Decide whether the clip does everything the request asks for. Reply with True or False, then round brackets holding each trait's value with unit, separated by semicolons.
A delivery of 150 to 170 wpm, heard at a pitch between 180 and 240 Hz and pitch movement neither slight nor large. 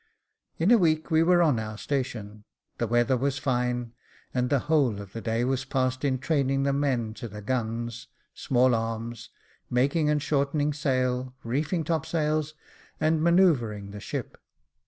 False (160 wpm; 130 Hz; 4.3 semitones)